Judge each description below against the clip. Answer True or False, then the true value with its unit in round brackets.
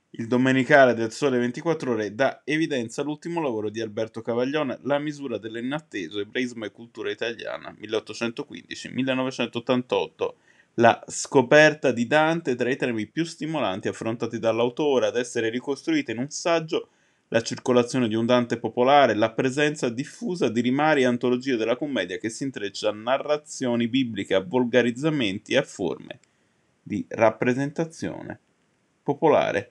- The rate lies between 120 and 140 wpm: True (135 wpm)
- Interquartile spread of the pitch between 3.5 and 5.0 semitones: True (4.0 semitones)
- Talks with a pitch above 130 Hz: False (125 Hz)